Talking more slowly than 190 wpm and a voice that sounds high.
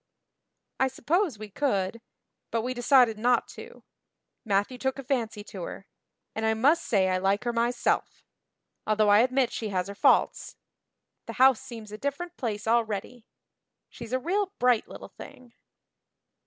Yes: average, 155 wpm; high, 235 Hz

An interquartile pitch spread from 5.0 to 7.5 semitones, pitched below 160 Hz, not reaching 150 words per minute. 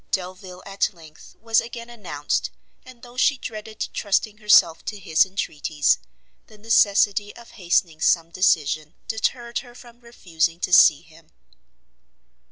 No: wide, 5.4 semitones; high, 195 Hz; slow, 135 wpm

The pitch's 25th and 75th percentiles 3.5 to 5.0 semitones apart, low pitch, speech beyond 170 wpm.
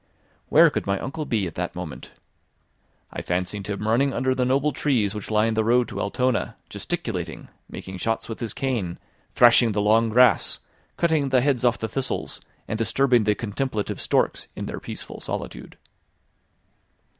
No: average, 3.9 semitones; low, 115 Hz; average, 165 wpm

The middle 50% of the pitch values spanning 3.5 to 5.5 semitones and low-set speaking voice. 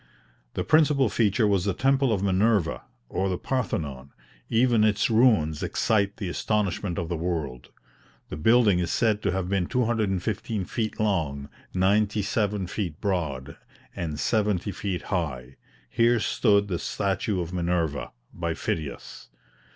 Yes: average, 4.2 semitones; low, 100 Hz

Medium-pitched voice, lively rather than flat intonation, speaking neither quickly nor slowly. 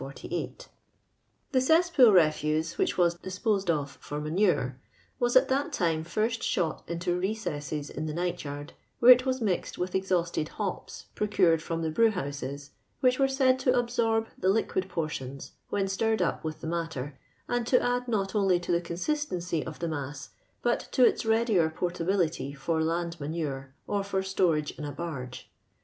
Yes: medium, 175 Hz; wide, 6.0 semitones; average, 170 wpm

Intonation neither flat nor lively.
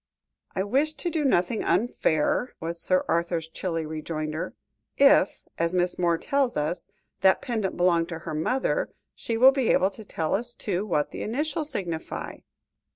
No: wide, 6.5 semitones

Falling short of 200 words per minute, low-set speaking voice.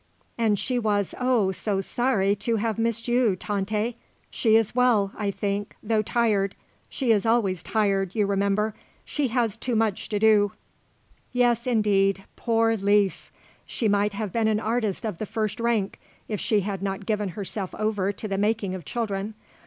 No: average, 170 wpm; high, 210 Hz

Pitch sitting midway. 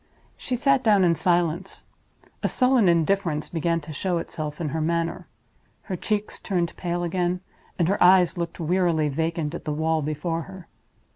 Yes: medium, 170 Hz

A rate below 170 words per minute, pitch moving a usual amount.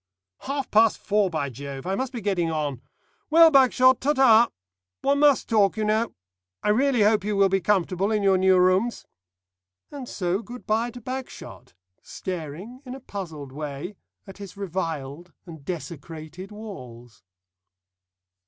No: average, 155 wpm; wide, 6.1 semitones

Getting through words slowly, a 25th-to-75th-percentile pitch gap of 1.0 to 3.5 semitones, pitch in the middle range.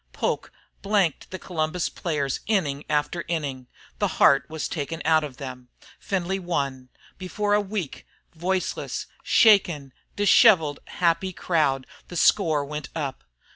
No: slow, 130 wpm; average, 4.7 semitones; medium, 160 Hz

